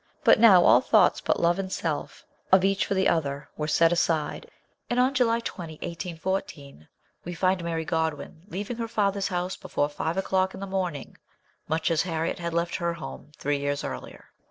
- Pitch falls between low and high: Yes, medium, 175 Hz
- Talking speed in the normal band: Yes, average, 185 wpm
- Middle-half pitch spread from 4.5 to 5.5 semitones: No, average, 3.1 semitones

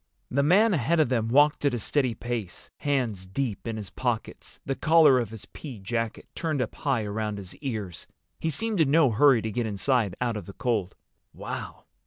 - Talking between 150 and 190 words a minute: No, average, 200 wpm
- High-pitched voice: No, low, 120 Hz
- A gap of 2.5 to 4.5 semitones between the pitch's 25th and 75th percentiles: No, average, 4.9 semitones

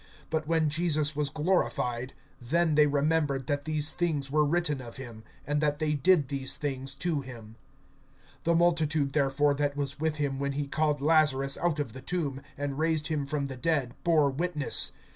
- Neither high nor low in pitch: Yes, medium, 145 Hz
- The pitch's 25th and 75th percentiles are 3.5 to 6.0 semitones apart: No, narrow, 2.4 semitones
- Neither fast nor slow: Yes, average, 180 wpm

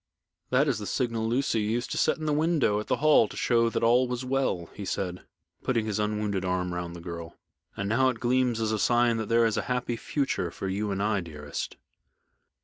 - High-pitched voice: No, low, 110 Hz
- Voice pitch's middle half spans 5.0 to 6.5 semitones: No, average, 4.2 semitones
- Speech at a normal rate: No, fast, 225 wpm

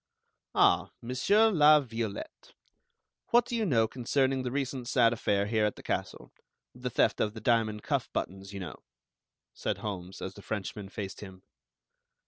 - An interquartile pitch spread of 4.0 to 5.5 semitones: Yes, average, 4.5 semitones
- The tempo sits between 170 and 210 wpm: No, average, 160 wpm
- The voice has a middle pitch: No, low, 115 Hz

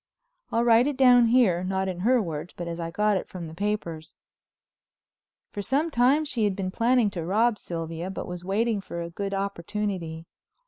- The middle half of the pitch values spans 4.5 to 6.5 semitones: Yes, average, 5.2 semitones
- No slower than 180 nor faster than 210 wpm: Yes, average, 190 wpm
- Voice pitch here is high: Yes, high, 200 Hz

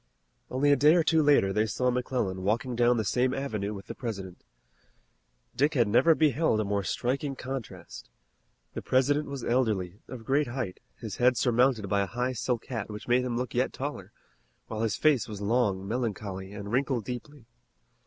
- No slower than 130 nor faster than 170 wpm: No, average, 185 wpm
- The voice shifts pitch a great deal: No, average, 4.1 semitones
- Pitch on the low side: Yes, low, 120 Hz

